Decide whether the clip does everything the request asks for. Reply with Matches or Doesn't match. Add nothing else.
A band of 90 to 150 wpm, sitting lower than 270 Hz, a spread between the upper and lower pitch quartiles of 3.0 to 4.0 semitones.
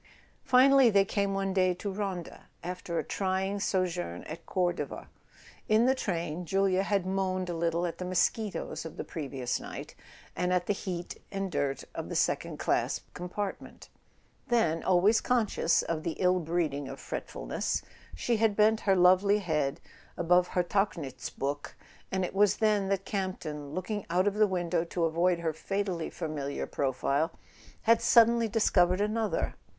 Doesn't match